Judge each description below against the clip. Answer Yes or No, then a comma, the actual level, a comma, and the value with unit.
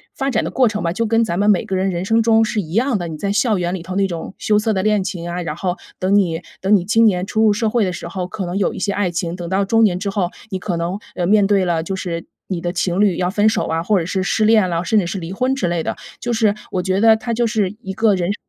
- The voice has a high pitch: Yes, high, 195 Hz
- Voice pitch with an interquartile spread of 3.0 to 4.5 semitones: Yes, average, 3.3 semitones